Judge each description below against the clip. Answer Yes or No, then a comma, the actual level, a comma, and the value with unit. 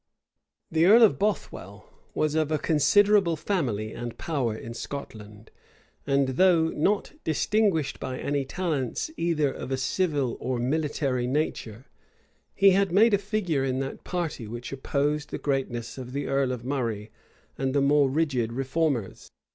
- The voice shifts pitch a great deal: No, average, 4.6 semitones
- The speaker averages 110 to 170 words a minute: Yes, average, 150 wpm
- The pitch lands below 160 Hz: Yes, medium, 140 Hz